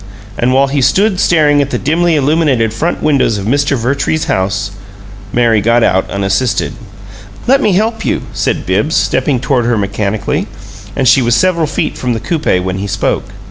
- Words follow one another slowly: No, average, 180 wpm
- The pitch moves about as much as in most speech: No, wide, 5.9 semitones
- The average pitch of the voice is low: Yes, low, 130 Hz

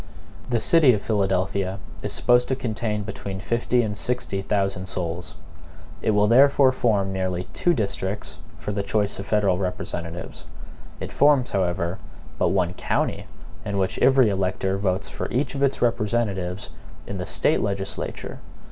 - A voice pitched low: Yes, low, 100 Hz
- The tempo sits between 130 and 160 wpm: Yes, average, 150 wpm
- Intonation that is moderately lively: Yes, average, 3.9 semitones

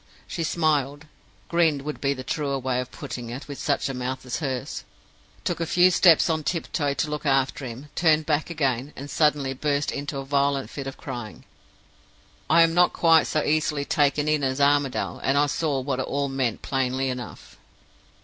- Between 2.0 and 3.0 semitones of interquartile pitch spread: Yes, narrow, 2.4 semitones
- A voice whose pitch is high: No, medium, 140 Hz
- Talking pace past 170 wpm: Yes, average, 190 wpm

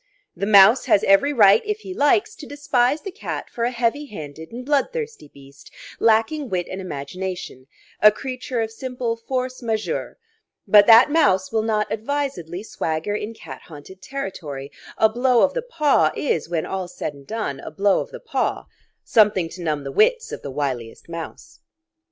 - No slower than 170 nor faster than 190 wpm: Yes, average, 175 wpm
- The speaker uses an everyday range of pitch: No, wide, 7.4 semitones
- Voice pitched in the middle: No, high, 220 Hz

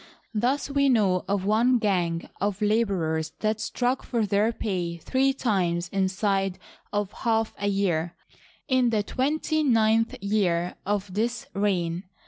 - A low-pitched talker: No, high, 205 Hz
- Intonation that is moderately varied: Yes, average, 3.8 semitones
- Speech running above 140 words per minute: No, slow, 135 wpm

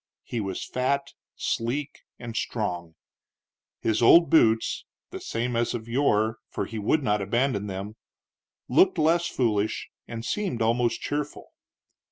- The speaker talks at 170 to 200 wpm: No, slow, 135 wpm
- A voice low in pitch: Yes, low, 115 Hz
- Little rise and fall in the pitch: No, average, 4.3 semitones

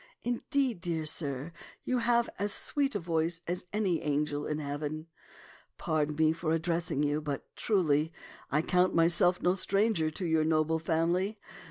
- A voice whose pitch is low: No, medium, 165 Hz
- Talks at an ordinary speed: Yes, average, 155 wpm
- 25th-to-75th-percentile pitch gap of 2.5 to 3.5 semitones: Yes, average, 3.1 semitones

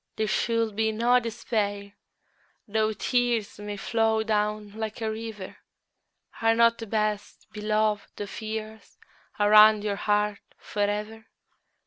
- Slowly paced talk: Yes, slow, 125 wpm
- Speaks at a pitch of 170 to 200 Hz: No, high, 215 Hz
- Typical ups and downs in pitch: No, narrow, 1.2 semitones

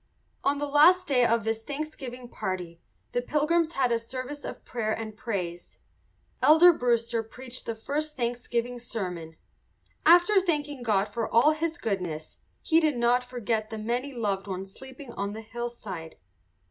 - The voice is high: Yes, high, 240 Hz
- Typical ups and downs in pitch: Yes, average, 4.9 semitones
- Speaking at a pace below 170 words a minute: Yes, average, 155 wpm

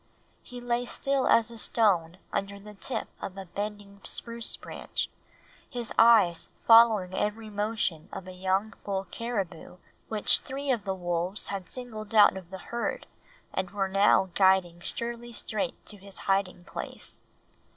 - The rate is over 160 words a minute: No, average, 150 wpm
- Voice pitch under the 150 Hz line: No, high, 205 Hz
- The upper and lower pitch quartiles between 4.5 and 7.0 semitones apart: No, average, 3.3 semitones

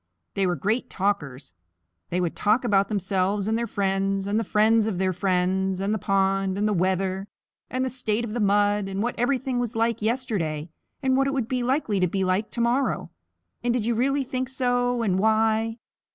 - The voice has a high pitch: Yes, high, 210 Hz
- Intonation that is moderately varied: Yes, average, 3.9 semitones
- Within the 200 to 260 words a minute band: Yes, fast, 205 wpm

